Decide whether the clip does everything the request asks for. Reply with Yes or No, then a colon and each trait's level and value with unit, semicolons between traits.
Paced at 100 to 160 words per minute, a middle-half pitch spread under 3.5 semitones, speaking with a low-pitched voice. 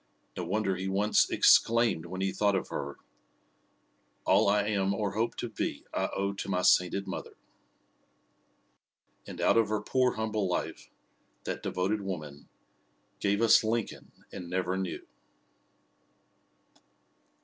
Yes: slow, 135 wpm; average, 2.7 semitones; low, 100 Hz